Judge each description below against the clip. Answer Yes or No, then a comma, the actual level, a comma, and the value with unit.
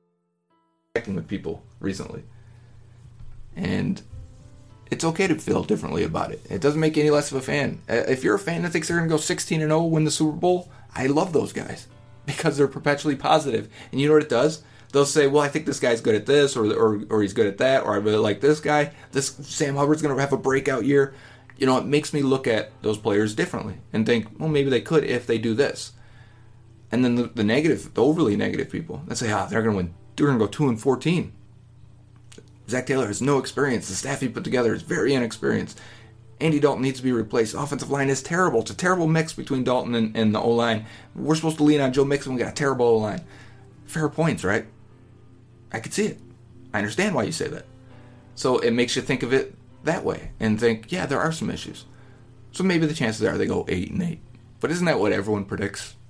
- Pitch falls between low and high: No, low, 130 Hz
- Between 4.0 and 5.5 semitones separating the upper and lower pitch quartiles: Yes, average, 4.3 semitones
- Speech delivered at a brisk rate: Yes, fast, 230 wpm